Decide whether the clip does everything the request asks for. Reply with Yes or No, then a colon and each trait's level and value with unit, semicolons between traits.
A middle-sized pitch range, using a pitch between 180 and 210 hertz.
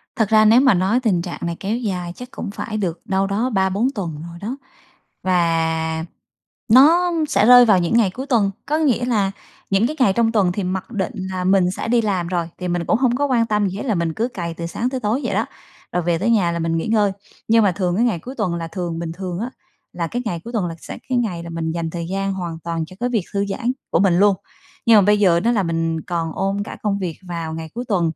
Yes: average, 4.9 semitones; high, 195 Hz